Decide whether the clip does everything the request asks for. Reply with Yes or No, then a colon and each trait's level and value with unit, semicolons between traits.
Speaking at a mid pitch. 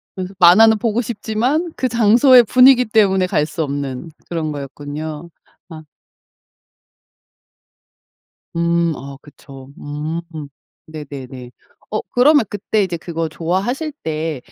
Yes: medium, 170 Hz